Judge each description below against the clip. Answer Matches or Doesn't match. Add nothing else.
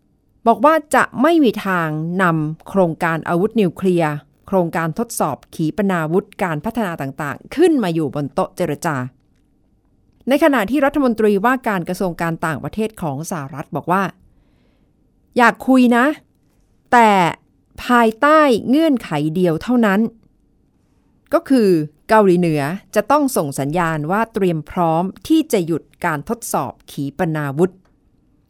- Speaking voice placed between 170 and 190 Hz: Matches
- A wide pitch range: Matches